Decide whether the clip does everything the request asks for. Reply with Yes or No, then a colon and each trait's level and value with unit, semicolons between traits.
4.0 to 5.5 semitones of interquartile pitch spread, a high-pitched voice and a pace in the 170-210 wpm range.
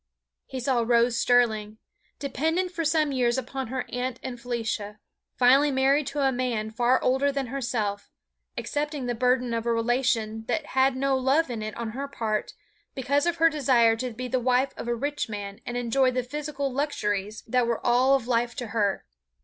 No: average, 2.8 semitones; very high, 250 Hz; average, 190 wpm